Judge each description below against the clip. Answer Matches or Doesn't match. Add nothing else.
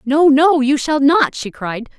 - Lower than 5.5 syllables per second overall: Matches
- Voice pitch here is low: Doesn't match